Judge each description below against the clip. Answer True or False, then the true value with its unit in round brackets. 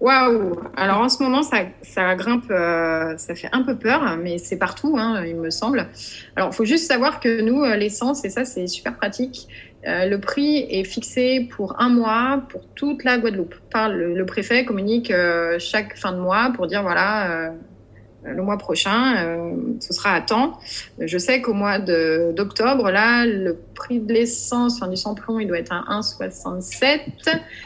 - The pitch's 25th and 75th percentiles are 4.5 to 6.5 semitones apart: True (5.3 semitones)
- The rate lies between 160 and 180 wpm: True (175 wpm)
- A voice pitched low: False (210 Hz)